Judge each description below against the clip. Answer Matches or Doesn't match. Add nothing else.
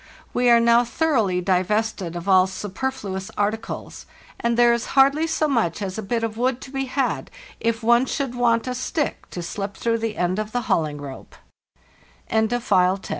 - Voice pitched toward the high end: Matches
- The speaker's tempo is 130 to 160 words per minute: Doesn't match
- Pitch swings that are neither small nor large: Matches